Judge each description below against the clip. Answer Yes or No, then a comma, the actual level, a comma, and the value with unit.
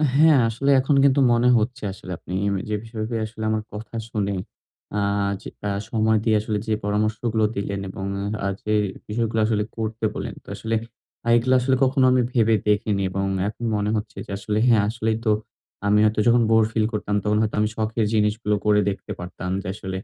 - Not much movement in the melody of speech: Yes, narrow, 1.6 semitones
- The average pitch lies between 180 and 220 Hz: No, low, 110 Hz